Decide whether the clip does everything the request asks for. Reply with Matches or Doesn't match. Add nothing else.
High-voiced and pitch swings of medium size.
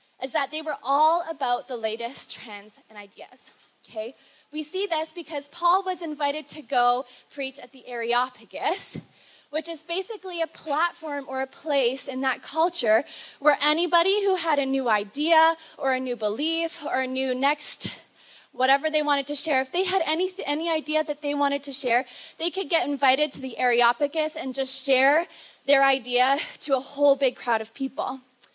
Matches